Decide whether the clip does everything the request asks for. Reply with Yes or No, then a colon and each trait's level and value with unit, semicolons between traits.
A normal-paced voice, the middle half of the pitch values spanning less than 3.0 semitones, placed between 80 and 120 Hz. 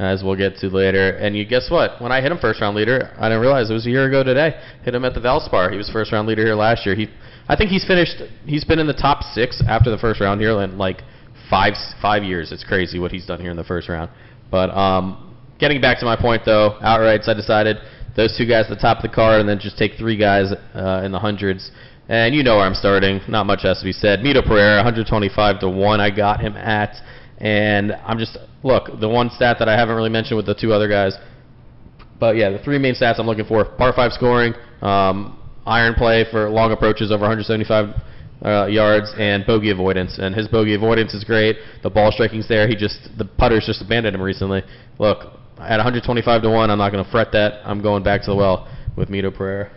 No: fast, 240 wpm; narrow, 2.5 semitones; low, 110 Hz